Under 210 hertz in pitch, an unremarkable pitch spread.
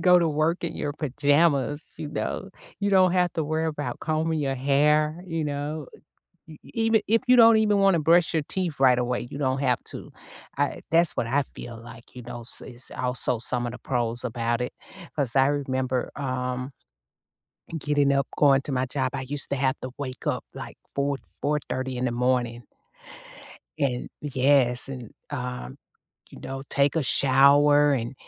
Yes: medium, 140 Hz; average, 3.4 semitones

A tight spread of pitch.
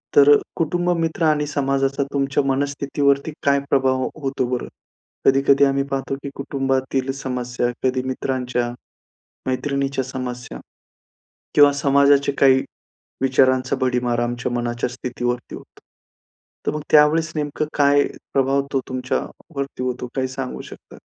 Yes: narrow, 1.6 semitones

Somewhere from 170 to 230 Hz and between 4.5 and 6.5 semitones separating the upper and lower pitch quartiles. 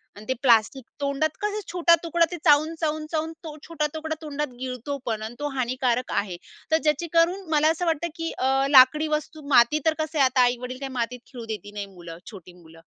No: very high, 280 Hz; average, 4.8 semitones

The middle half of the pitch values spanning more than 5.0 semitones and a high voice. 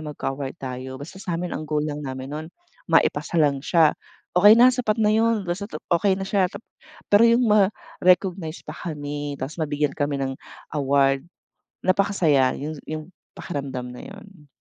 No: wide, 5.4 semitones; medium, 155 Hz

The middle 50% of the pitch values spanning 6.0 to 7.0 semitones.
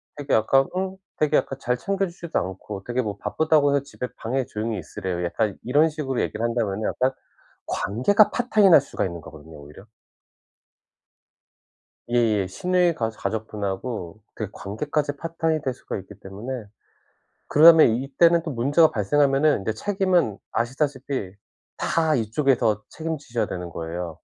Yes: wide, 6.6 semitones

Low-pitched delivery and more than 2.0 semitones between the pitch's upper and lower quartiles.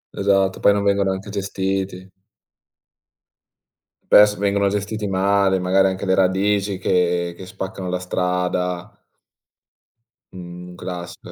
No: very low, 95 Hz; narrow, 1.6 semitones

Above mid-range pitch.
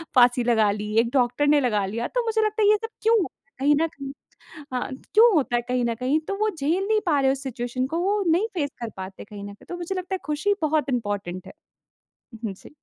Yes: very high, 275 Hz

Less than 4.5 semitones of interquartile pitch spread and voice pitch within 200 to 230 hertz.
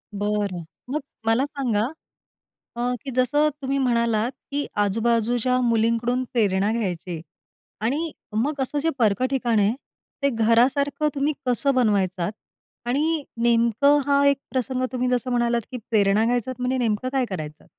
No: average, 3.7 semitones; high, 240 Hz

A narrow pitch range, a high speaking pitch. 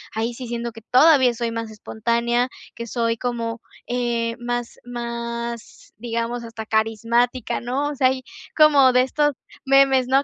Yes: narrow, 1.8 semitones; high, 240 Hz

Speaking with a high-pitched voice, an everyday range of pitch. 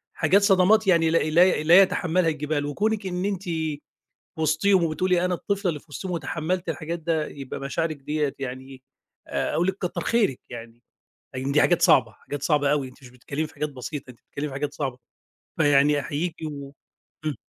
No: medium, 155 Hz; average, 4.1 semitones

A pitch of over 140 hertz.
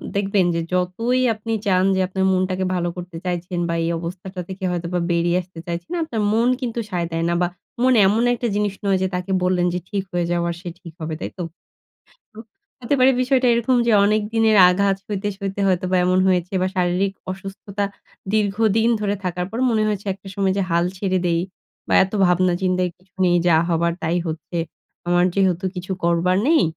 Yes: medium, 185 Hz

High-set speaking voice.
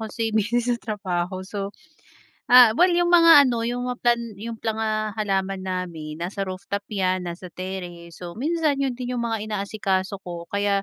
Yes: high, 205 Hz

